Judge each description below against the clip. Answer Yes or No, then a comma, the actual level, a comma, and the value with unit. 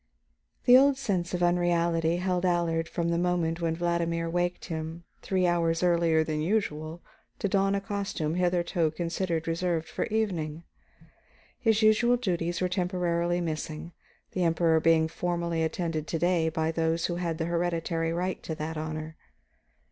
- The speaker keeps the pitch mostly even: Yes, narrow, 1.6 semitones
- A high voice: No, medium, 170 Hz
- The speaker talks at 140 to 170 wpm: Yes, average, 155 wpm